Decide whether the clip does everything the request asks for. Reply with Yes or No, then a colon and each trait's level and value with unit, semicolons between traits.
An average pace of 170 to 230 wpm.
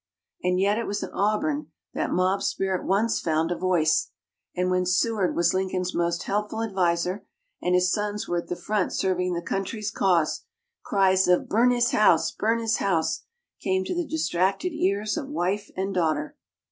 Yes: average, 175 wpm